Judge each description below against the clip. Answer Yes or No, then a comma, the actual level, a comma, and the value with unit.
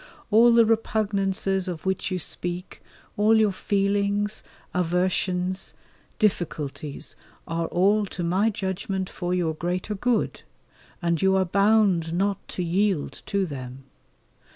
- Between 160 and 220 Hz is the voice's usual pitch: Yes, high, 190 Hz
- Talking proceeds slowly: Yes, slow, 125 wpm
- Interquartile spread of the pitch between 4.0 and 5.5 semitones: No, narrow, 2.6 semitones